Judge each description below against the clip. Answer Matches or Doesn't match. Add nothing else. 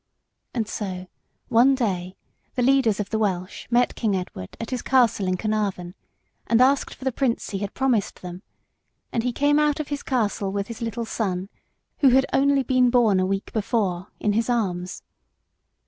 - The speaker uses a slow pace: Doesn't match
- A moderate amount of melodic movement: Matches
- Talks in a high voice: Matches